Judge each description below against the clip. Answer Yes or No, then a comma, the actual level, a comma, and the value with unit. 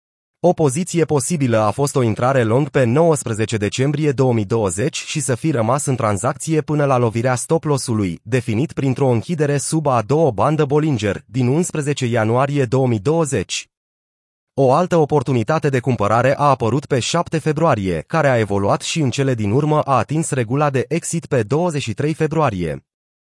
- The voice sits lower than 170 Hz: Yes, low, 135 Hz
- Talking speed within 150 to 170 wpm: Yes, average, 155 wpm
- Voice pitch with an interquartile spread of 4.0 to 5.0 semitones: Yes, average, 4.3 semitones